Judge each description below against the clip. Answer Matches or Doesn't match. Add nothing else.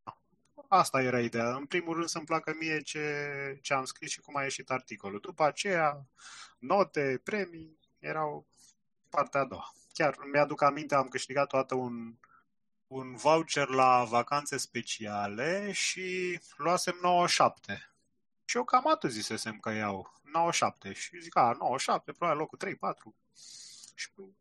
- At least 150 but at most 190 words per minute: Doesn't match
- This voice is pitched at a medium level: Matches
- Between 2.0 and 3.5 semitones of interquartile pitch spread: Doesn't match